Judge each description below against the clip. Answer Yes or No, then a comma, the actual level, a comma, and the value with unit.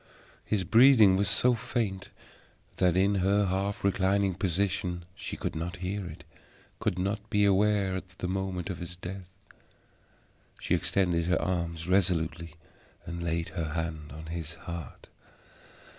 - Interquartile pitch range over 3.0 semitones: No, average, 2.7 semitones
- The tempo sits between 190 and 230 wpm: No, average, 145 wpm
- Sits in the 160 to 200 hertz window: No, very low, 95 Hz